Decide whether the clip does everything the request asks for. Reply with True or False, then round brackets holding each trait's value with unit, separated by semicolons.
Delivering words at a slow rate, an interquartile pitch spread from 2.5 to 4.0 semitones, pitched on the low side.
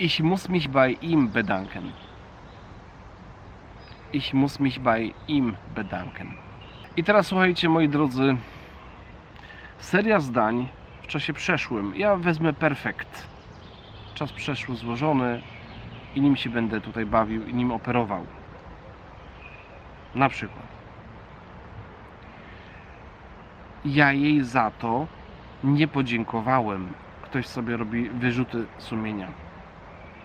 False (100 wpm; 4.7 semitones; 120 Hz)